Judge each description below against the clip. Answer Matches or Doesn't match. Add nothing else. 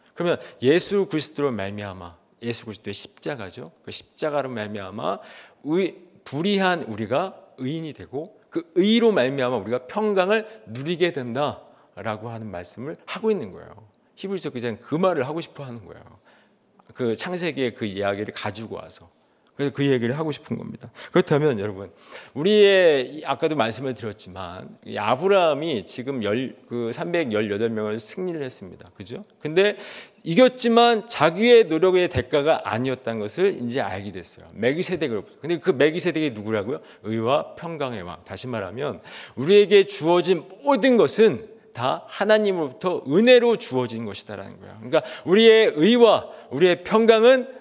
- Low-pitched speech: Doesn't match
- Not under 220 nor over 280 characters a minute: Doesn't match